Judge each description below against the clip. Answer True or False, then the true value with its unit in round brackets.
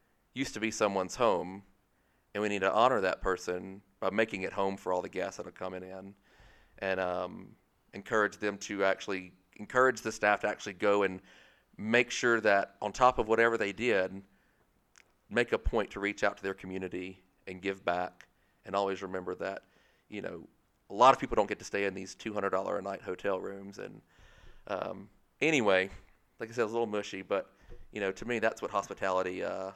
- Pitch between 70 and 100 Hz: True (95 Hz)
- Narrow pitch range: True (1.8 semitones)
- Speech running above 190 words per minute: True (200 wpm)